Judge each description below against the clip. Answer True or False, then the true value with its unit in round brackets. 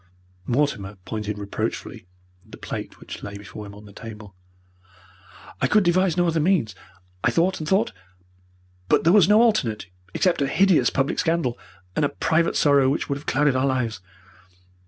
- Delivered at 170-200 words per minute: True (175 wpm)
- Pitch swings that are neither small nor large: False (8.1 semitones)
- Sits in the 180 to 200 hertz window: False (140 Hz)